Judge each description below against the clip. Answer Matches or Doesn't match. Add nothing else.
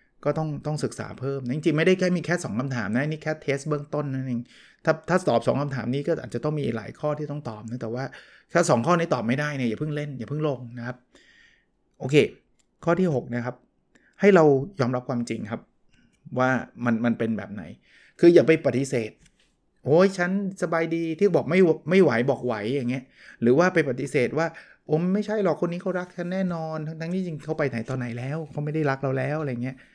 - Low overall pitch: Doesn't match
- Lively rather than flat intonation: Doesn't match